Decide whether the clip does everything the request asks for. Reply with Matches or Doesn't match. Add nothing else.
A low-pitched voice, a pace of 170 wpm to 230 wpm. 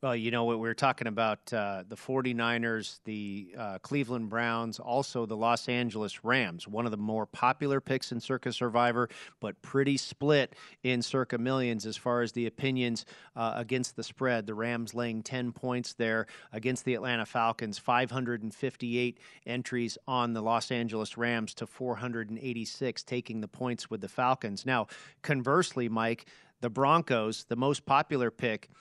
Doesn't match